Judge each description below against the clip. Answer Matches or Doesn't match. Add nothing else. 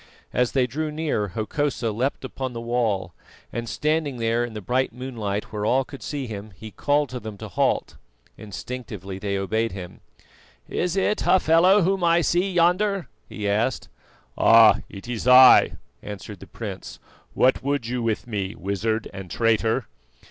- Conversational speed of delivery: Matches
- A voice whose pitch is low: Matches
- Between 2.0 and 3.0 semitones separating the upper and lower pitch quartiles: Doesn't match